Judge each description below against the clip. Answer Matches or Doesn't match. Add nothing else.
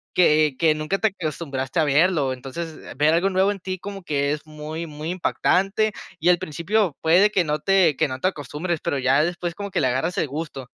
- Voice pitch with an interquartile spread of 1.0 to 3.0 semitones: Doesn't match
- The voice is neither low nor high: Matches